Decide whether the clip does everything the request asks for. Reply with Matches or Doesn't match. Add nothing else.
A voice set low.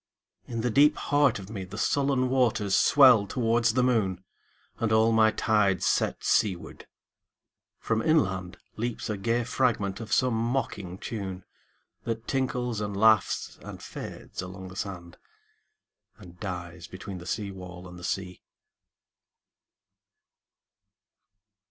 Matches